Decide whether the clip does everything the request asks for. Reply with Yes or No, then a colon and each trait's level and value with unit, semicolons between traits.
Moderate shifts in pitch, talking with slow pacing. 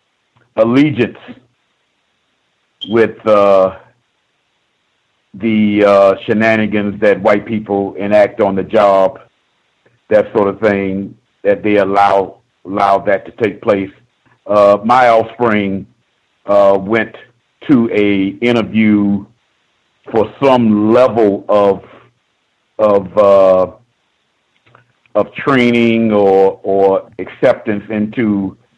No: narrow, 2.3 semitones; slow, 95 wpm